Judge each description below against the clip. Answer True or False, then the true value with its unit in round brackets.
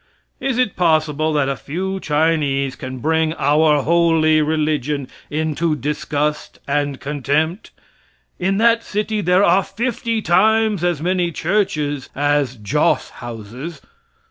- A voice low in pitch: False (155 Hz)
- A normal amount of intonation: True (3.9 semitones)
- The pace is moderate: False (120 wpm)